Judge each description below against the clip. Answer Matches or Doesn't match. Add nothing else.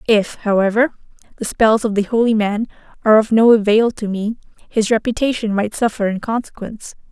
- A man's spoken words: Doesn't match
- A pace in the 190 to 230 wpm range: Doesn't match